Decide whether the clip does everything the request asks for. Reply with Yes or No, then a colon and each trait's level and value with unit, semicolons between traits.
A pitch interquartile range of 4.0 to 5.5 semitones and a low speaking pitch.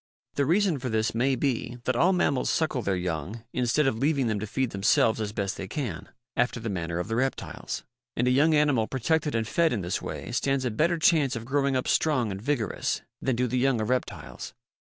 Yes: average, 4.5 semitones; low, 125 Hz